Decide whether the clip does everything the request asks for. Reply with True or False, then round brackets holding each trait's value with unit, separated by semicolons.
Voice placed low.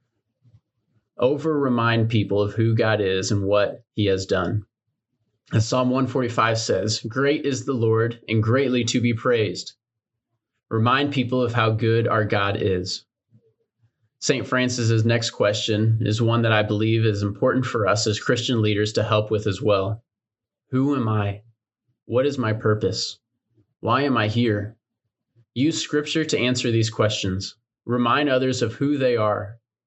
True (115 Hz)